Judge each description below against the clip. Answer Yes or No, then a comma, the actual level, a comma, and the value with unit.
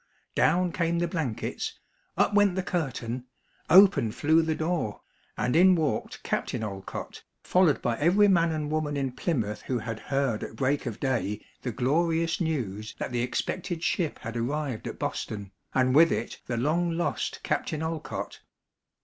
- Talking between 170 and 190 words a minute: No, average, 160 wpm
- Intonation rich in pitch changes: Yes, wide, 5.9 semitones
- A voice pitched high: No, medium, 150 Hz